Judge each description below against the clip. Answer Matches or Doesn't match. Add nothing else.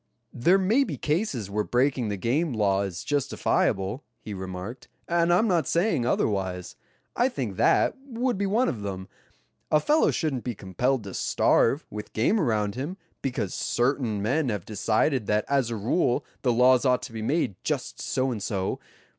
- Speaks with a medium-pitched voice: Doesn't match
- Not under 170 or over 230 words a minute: Matches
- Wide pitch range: Matches